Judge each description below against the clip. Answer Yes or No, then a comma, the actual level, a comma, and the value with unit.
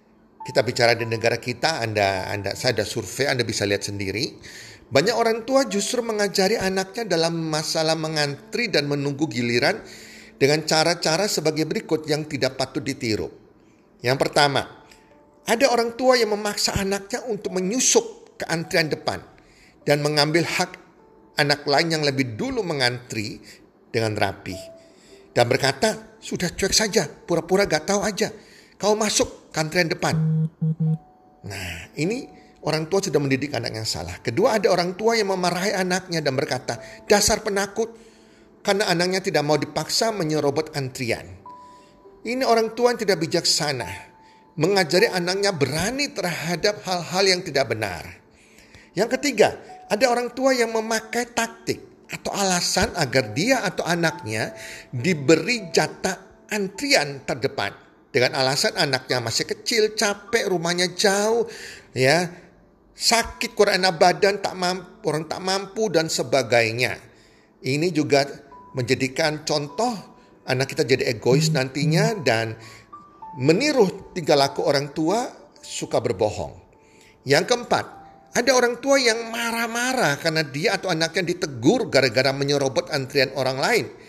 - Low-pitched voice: No, medium, 165 Hz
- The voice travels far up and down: Yes, wide, 7.2 semitones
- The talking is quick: No, average, 130 wpm